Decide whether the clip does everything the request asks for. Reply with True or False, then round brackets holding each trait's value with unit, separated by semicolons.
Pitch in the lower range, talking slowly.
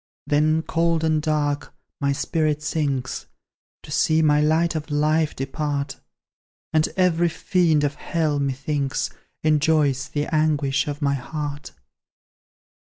False (150 Hz; 120 wpm)